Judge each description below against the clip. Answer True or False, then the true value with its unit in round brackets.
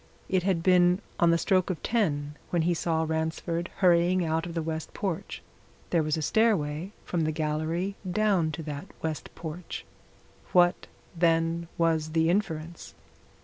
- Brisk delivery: False (155 wpm)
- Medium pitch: True (165 Hz)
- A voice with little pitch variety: True (2.0 semitones)